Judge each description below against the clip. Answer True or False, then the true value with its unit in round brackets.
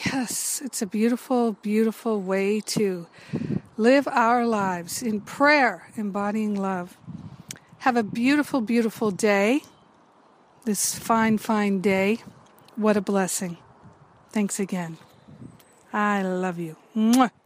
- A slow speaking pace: True (110 wpm)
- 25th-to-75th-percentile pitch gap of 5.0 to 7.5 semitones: False (3.2 semitones)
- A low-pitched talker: False (210 Hz)